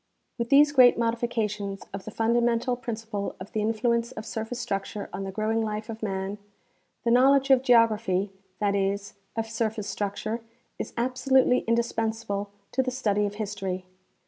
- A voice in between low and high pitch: No, high, 225 Hz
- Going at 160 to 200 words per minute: Yes, average, 170 wpm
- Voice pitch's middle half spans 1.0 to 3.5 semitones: Yes, average, 2.8 semitones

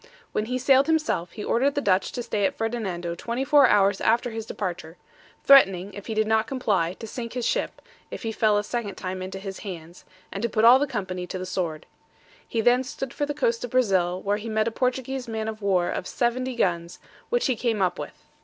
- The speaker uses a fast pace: Yes, fast, 225 wpm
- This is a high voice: Yes, high, 220 Hz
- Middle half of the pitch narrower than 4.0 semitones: No, average, 4.7 semitones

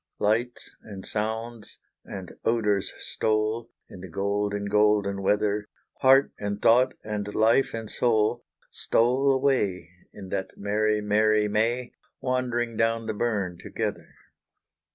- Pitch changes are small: Yes, narrow, 2.3 semitones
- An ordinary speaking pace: No, slow, 120 wpm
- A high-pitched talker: No, low, 110 Hz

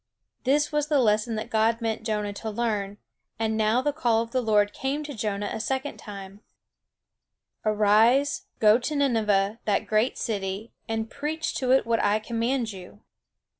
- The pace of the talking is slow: No, average, 170 wpm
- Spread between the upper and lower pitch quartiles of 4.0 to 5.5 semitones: No, average, 3.4 semitones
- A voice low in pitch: No, high, 225 Hz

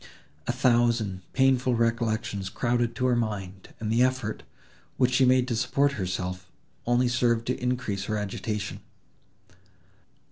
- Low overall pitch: Yes, low, 120 Hz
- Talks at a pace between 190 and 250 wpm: No, slow, 135 wpm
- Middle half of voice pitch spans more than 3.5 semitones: No, average, 3.0 semitones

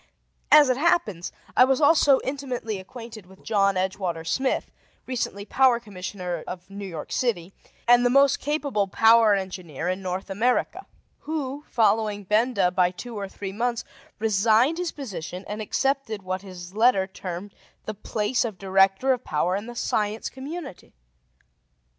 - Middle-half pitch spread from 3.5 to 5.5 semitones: Yes, average, 4.9 semitones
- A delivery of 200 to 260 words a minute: No, average, 150 wpm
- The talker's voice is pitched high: Yes, high, 210 Hz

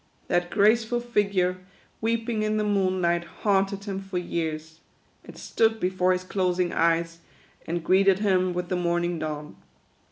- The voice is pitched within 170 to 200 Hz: Yes, medium, 185 Hz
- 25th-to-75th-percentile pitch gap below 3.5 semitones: Yes, average, 2.9 semitones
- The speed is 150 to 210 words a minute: No, average, 140 wpm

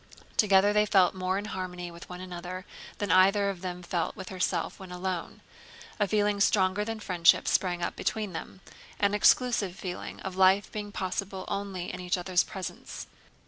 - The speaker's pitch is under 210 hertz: Yes, high, 190 Hz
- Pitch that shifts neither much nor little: No, narrow, 2.0 semitones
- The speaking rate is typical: Yes, average, 175 wpm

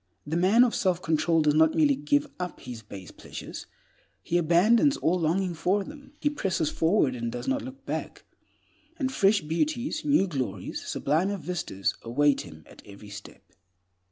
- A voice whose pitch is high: No, medium, 170 Hz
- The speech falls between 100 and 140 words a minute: No, average, 165 wpm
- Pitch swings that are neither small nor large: No, wide, 6.2 semitones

